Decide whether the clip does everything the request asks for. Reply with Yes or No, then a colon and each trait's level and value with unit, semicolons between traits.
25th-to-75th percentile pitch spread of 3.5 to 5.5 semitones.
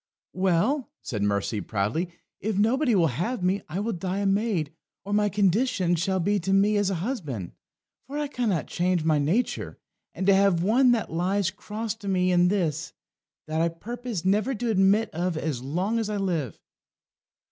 Yes: average, 4.2 semitones